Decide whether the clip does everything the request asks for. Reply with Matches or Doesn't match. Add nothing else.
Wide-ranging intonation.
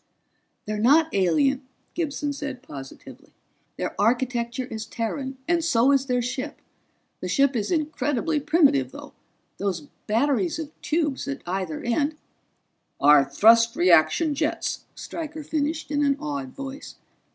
Matches